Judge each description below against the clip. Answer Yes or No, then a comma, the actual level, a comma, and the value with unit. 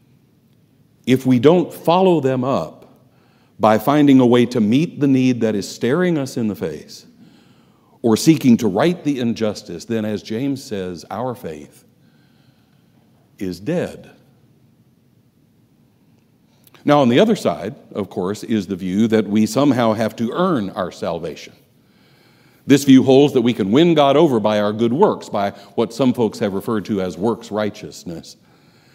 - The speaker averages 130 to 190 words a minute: Yes, average, 160 wpm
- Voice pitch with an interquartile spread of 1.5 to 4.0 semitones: No, average, 4.5 semitones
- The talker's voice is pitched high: No, low, 120 Hz